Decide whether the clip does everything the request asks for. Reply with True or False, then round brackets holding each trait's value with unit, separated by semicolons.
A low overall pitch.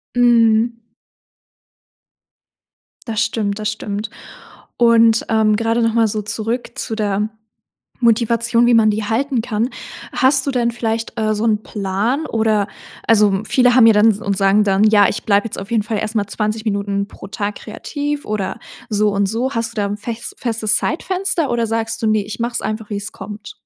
False (220 Hz)